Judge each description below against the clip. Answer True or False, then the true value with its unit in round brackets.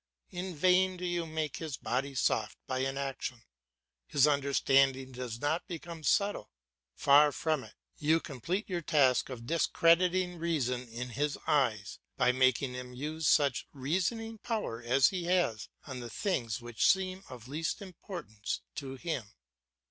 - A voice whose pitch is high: False (145 Hz)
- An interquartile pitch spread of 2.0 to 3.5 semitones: False (5.3 semitones)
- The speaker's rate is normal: True (150 wpm)